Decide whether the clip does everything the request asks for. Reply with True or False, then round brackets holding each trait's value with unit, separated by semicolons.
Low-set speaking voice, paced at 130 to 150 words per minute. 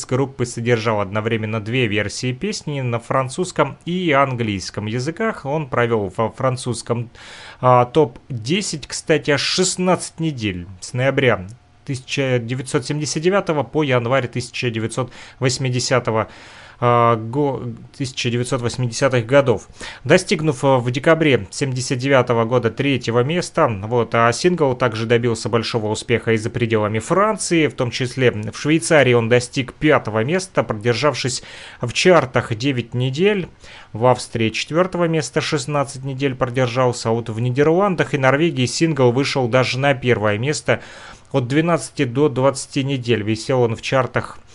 False (130 Hz; 120 wpm)